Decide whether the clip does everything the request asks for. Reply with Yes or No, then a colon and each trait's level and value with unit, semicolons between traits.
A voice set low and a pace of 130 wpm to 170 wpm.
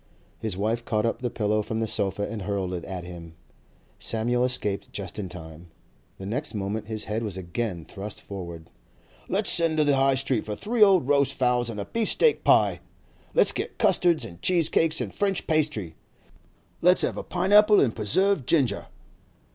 No: low, 110 Hz; average, 185 wpm